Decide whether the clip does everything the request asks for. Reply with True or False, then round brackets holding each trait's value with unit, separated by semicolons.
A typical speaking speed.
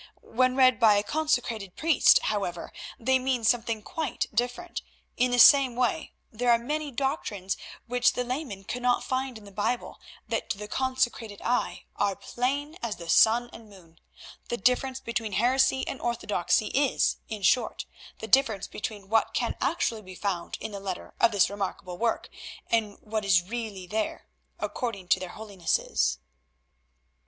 True (160 wpm)